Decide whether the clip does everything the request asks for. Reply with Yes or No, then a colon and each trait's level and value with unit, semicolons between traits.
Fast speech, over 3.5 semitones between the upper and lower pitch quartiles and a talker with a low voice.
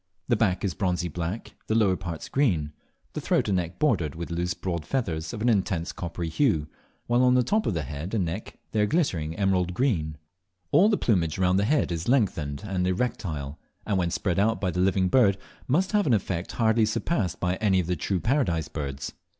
Yes: fast, 210 wpm; average, 4.9 semitones; very low, 95 Hz